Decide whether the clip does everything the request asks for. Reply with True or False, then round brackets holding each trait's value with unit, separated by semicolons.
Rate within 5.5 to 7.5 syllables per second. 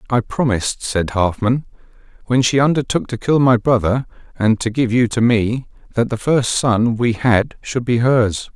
False (4.5 syllables/s)